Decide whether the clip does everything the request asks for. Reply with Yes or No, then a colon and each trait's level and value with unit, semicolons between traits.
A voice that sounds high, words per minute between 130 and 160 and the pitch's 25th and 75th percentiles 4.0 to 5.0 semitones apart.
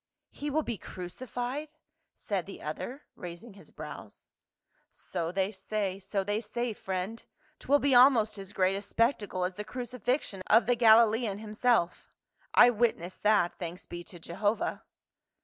Yes: high, 215 Hz; average, 150 wpm; average, 4.3 semitones